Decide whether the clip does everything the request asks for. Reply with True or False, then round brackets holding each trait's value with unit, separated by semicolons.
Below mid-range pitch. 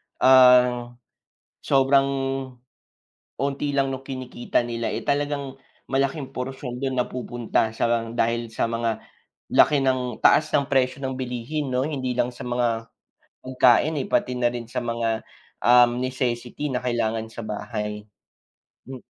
True (125 Hz)